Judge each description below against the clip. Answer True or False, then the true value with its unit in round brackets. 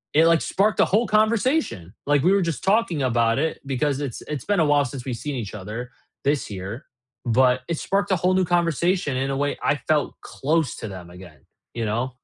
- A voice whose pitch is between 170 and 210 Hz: False (145 Hz)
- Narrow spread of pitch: False (6.4 semitones)